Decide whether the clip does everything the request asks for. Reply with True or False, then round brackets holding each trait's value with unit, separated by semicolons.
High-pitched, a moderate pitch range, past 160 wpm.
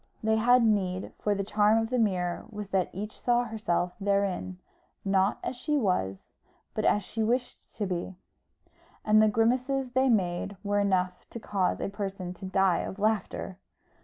True (205 Hz; 3.1 semitones; 170 wpm)